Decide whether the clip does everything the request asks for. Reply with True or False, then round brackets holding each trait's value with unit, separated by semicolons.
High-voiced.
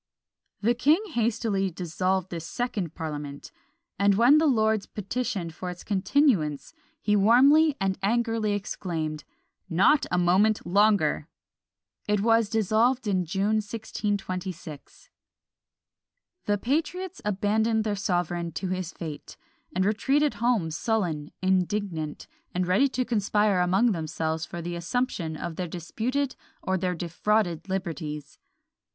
True (195 Hz)